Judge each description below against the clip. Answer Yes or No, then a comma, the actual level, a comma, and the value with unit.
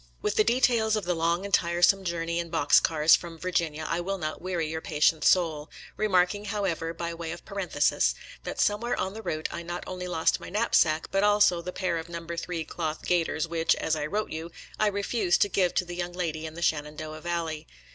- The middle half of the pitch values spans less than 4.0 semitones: Yes, average, 2.9 semitones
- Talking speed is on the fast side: Yes, fast, 230 wpm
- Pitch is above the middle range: No, medium, 170 Hz